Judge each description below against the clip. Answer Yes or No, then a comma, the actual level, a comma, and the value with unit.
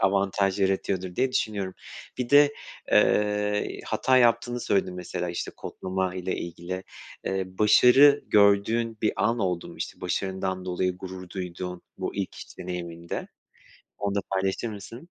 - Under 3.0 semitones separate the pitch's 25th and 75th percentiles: Yes, narrow, 2.5 semitones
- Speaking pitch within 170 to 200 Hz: No, very low, 95 Hz